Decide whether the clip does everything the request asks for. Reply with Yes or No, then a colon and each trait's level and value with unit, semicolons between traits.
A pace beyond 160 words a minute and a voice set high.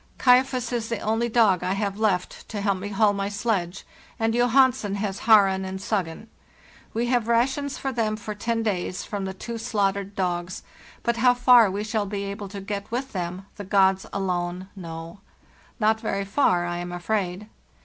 Yes: average, 190 wpm; high, 205 Hz